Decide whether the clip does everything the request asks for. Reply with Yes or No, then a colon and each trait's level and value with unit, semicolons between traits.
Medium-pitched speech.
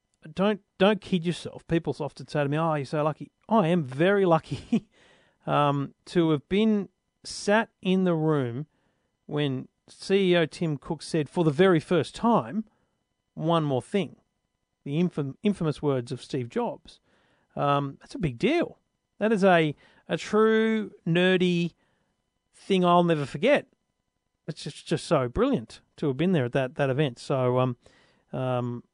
Yes: medium, 165 Hz